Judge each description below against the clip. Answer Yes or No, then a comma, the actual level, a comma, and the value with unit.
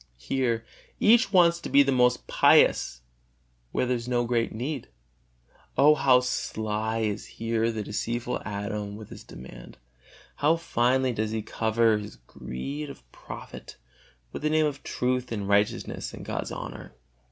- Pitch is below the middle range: Yes, low, 115 Hz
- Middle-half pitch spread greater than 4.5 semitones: No, average, 3.7 semitones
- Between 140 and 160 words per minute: Yes, average, 150 wpm